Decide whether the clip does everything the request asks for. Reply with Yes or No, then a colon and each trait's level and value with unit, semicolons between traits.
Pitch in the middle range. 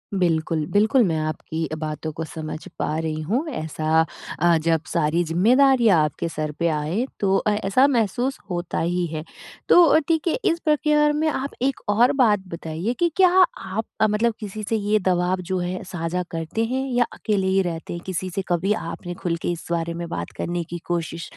Yes: medium, 180 Hz